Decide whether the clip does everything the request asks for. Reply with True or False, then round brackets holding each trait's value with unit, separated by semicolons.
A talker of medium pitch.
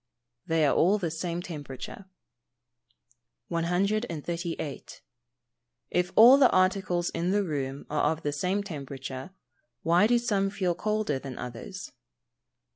True (175 Hz)